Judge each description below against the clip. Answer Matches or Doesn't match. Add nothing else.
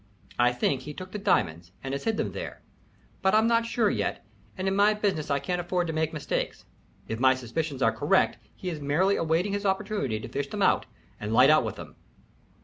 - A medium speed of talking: Doesn't match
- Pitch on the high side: Doesn't match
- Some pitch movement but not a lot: Doesn't match